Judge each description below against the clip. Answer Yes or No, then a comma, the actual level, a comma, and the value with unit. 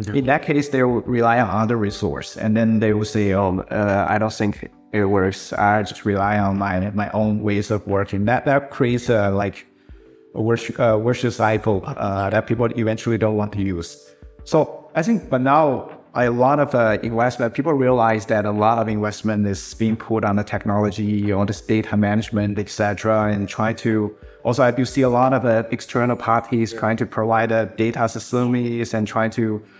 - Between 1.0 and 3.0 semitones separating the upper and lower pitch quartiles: Yes, narrow, 2.4 semitones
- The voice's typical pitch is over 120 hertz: No, low, 110 Hz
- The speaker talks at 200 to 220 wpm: Yes, fast, 205 wpm